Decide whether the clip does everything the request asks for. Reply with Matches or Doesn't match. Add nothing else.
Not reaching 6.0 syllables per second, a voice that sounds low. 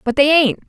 Doesn't match